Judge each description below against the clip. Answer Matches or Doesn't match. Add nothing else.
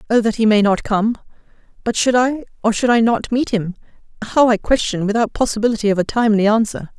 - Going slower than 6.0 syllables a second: Doesn't match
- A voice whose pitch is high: Matches